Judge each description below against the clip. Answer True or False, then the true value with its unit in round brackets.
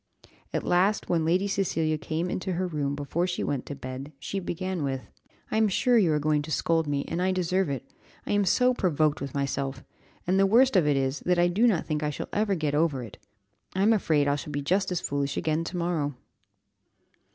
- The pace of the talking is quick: True (220 wpm)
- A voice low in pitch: False (165 Hz)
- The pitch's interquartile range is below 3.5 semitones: False (4.5 semitones)